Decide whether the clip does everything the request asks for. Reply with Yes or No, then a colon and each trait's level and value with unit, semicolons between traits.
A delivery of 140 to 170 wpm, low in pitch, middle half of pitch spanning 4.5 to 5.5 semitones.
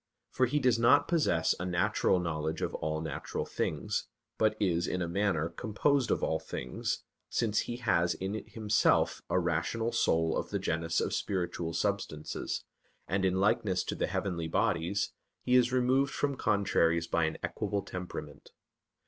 Yes: average, 160 wpm; very low, 95 Hz; average, 5.2 semitones